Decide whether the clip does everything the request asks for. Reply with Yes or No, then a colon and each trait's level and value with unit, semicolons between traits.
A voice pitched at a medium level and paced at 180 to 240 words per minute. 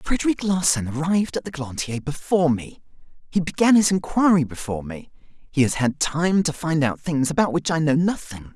Yes: medium, 155 Hz; average, 190 wpm